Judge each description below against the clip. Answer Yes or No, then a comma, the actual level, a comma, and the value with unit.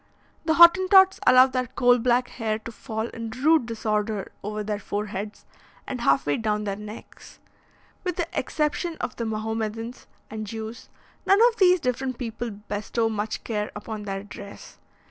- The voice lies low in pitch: No, high, 225 Hz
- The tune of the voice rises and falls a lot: No, average, 3.3 semitones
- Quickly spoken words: No, average, 160 wpm